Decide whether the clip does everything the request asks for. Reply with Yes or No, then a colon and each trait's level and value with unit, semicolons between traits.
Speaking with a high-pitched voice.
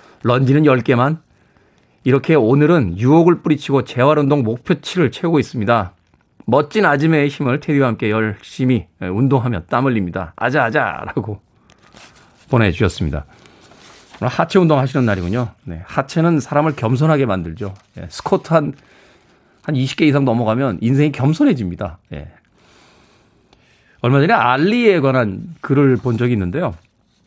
No: low, 130 Hz